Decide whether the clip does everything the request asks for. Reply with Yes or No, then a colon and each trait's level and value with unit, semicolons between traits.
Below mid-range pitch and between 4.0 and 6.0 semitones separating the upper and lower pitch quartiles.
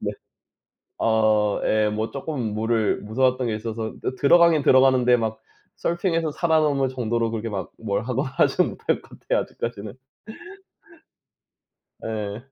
No: low, 115 Hz; average, 3.5 semitones